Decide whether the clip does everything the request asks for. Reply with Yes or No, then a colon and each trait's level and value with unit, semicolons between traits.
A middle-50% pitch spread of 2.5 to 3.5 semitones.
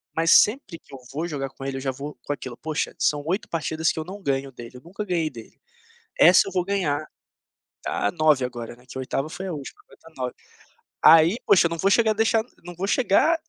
No: wide, 5.5 semitones